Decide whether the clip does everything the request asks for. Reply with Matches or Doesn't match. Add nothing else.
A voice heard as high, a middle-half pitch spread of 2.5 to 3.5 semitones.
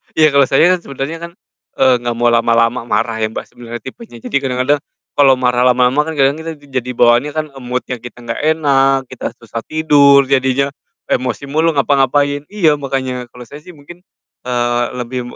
Doesn't match